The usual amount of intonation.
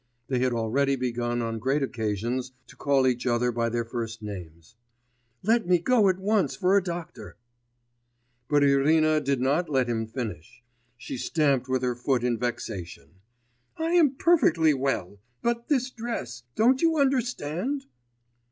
No: wide, 7.5 semitones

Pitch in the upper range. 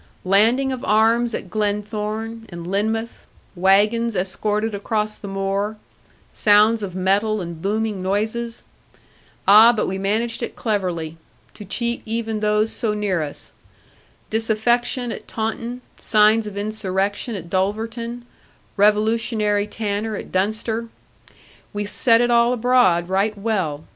Yes: high, 215 Hz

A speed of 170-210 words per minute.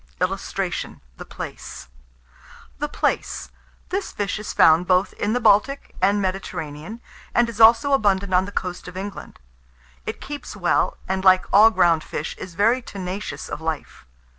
No: average, 160 wpm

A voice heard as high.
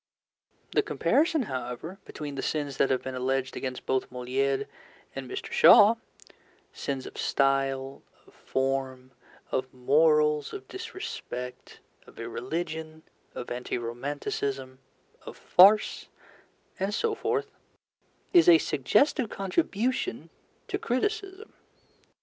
No: medium, 140 Hz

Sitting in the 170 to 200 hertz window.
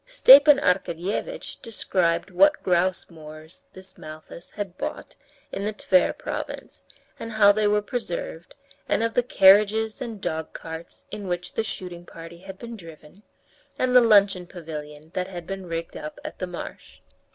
Yes: high, 190 Hz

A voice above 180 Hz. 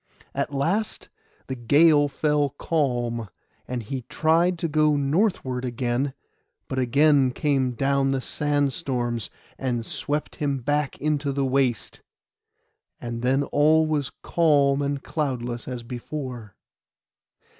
No: medium, 140 Hz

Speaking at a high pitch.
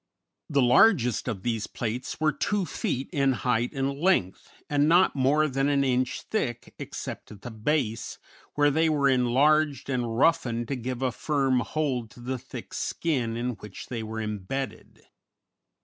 No: low, 130 Hz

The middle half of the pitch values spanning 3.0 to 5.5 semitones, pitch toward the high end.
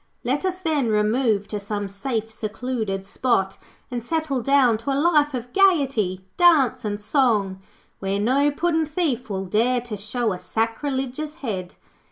Yes: average, 5.1 semitones; high, 245 Hz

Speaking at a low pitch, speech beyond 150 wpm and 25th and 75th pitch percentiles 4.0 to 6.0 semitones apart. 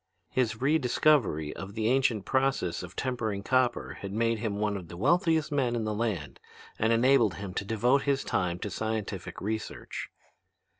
Yes: low, 110 Hz; average, 165 wpm; average, 4.4 semitones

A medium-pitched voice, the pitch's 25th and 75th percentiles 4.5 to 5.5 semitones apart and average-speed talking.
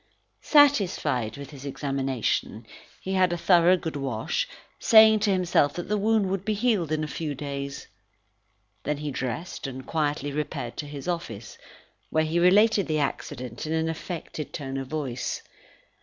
Yes: medium, 155 Hz; average, 4.9 semitones; average, 160 wpm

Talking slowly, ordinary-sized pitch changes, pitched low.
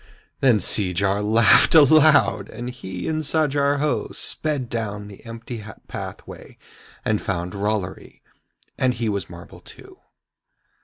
No: slow, 120 wpm; wide, 5.9 semitones; low, 115 Hz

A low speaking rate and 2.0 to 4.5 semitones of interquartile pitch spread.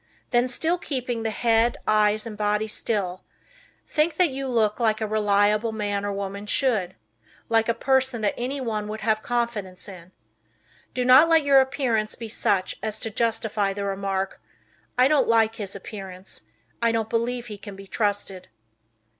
No: average, 165 wpm; average, 2.9 semitones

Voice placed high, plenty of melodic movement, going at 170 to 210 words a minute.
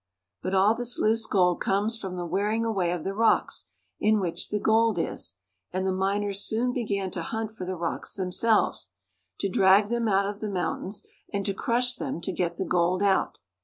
No: high, 200 Hz; average, 2.8 semitones; average, 200 wpm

